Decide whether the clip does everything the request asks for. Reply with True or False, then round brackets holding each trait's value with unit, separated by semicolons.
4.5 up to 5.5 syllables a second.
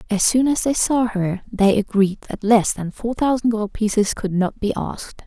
True (4.8 syllables/s)